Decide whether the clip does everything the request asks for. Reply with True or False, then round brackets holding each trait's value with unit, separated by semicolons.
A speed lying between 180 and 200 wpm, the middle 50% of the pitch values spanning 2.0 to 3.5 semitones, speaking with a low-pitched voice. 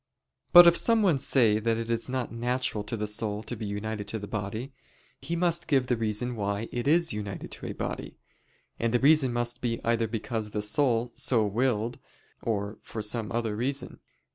True (190 wpm; 3.2 semitones; 115 Hz)